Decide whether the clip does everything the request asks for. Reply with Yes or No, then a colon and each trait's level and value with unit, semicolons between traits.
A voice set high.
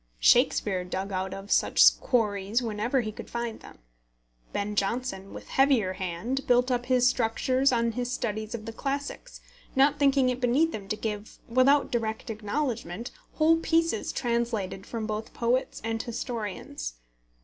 Yes: high, 230 Hz